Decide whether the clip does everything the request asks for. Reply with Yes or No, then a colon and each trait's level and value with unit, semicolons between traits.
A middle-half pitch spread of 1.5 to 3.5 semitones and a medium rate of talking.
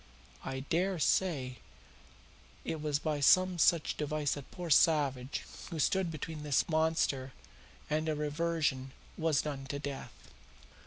No: average, 2.7 semitones; slow, 130 wpm